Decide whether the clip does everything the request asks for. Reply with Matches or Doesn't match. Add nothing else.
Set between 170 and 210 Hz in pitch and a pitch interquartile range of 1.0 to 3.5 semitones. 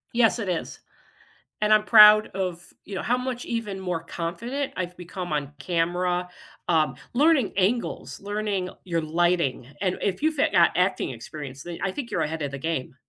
Doesn't match